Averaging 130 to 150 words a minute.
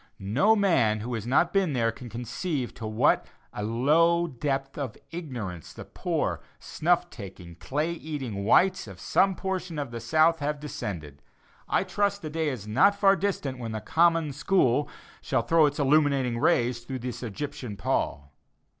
No: average, 165 wpm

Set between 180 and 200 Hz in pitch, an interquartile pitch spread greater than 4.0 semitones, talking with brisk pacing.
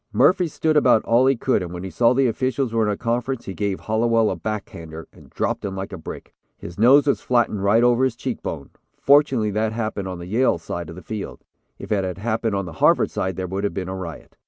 No: low, 110 Hz; average, 4.5 semitones; fast, 255 wpm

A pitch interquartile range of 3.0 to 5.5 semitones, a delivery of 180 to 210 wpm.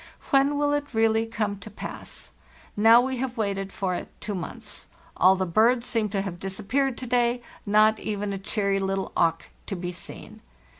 Yes: average, 3.7 semitones; average, 185 wpm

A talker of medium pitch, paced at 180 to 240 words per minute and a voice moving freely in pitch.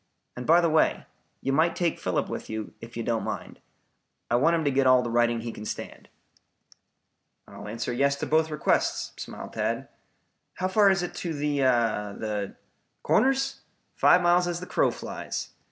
Yes: medium, 145 Hz; average, 185 wpm; wide, 6.5 semitones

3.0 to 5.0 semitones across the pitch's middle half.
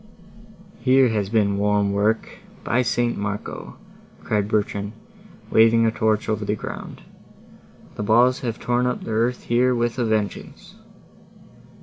No: narrow, 2.6 semitones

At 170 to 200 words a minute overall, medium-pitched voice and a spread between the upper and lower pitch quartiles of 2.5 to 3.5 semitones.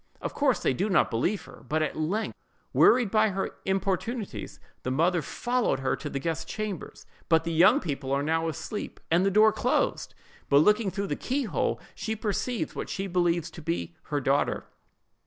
No: average, 185 wpm; medium, 180 Hz; average, 5.3 semitones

